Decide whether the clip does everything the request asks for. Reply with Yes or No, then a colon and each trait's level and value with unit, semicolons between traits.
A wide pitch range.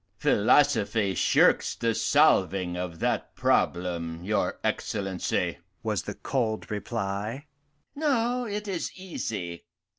Yes: wide, 8.3 semitones